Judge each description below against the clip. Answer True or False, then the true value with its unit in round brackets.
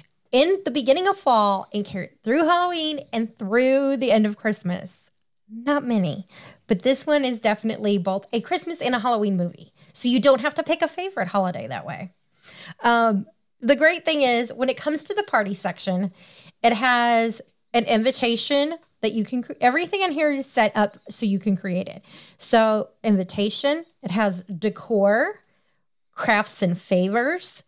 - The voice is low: False (230 Hz)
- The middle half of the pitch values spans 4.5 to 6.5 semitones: True (5.5 semitones)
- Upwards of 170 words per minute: False (165 wpm)